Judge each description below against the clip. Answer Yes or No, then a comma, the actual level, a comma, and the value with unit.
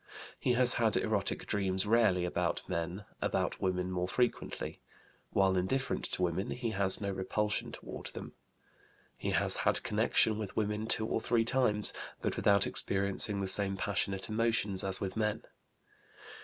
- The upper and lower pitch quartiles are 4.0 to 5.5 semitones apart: No, average, 2.7 semitones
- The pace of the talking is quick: No, average, 155 wpm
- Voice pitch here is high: No, low, 100 Hz